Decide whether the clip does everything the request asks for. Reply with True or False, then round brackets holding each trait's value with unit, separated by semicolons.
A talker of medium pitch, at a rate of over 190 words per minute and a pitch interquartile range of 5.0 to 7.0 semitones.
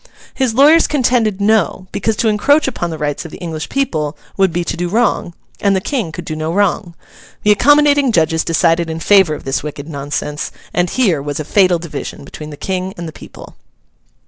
True (175 Hz; 200 wpm; 5.6 semitones)